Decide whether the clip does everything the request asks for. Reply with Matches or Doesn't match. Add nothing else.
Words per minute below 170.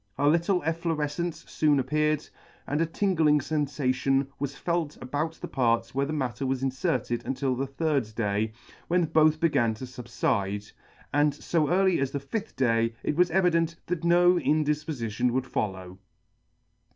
Matches